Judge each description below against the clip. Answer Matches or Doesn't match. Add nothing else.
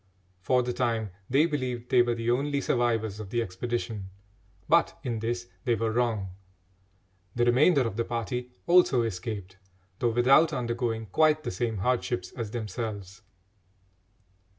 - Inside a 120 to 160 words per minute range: Matches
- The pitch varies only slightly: Matches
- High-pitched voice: Doesn't match